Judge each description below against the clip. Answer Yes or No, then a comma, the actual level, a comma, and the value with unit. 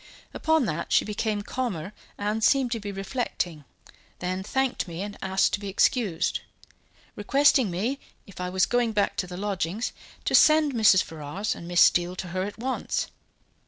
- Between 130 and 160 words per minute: No, average, 170 wpm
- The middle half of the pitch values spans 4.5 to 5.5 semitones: Yes, average, 4.8 semitones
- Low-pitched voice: No, high, 205 Hz